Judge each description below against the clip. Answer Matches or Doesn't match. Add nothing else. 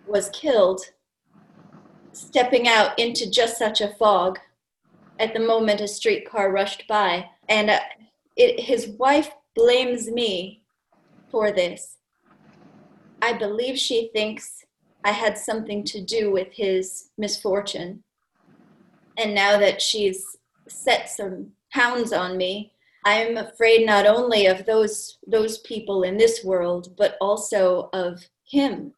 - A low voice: Doesn't match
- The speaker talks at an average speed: Doesn't match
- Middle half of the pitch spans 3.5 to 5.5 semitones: Doesn't match